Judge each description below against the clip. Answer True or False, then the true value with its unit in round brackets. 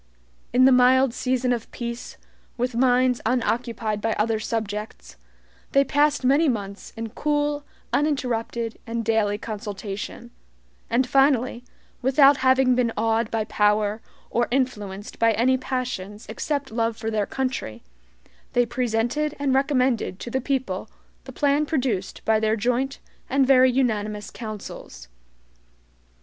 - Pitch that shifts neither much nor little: True (3.1 semitones)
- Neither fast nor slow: False (130 wpm)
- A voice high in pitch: True (240 Hz)